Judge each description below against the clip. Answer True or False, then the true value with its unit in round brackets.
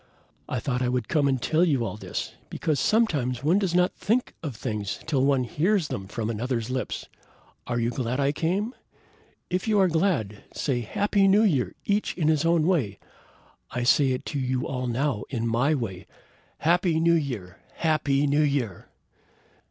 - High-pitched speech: False (140 Hz)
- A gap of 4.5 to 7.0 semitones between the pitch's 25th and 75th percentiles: True (5.6 semitones)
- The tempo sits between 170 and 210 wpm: True (180 wpm)